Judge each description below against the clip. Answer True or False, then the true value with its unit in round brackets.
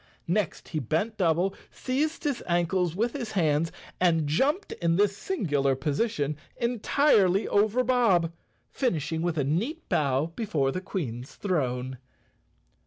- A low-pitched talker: False (175 Hz)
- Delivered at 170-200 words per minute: False (140 wpm)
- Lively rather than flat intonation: True (6.5 semitones)